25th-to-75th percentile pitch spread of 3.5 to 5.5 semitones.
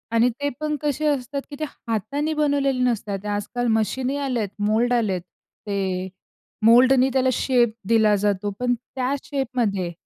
Yes: average, 4.5 semitones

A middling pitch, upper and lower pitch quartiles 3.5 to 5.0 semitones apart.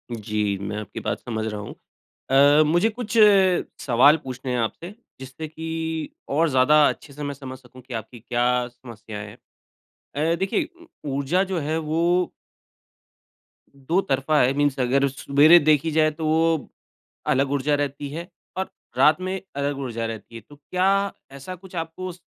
Yes: medium, 145 Hz; average, 4.3 semitones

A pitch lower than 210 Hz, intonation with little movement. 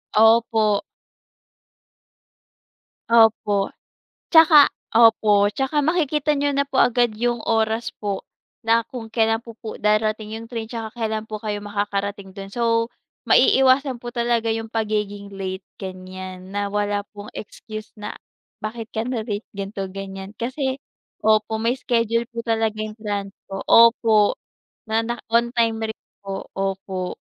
No: high, 220 Hz; narrow, 2.3 semitones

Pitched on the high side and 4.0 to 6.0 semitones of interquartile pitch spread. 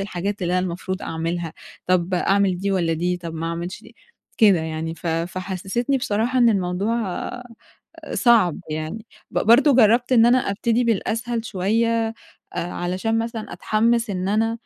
Yes: high, 200 Hz; average, 4.4 semitones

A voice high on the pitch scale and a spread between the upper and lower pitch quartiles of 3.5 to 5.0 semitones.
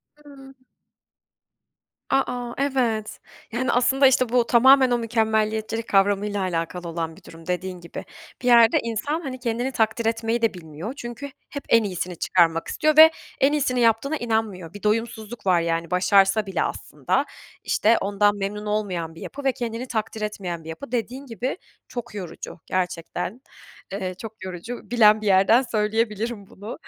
Yes: high, 220 Hz; average, 4.1 semitones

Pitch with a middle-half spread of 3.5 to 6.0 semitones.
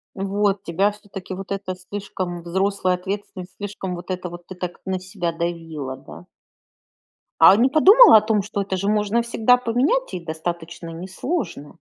No: average, 3.0 semitones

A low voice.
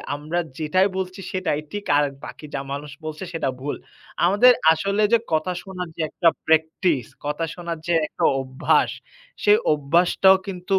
No: medium, 170 Hz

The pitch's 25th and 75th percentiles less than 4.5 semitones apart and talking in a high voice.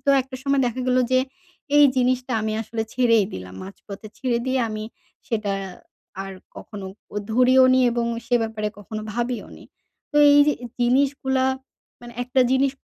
Yes: average, 3.1 semitones; high, 245 Hz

